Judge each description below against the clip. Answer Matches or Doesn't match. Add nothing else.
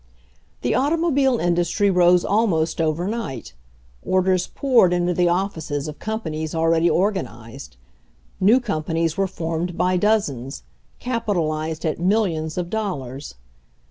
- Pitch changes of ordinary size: Matches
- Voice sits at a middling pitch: Matches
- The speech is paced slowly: Matches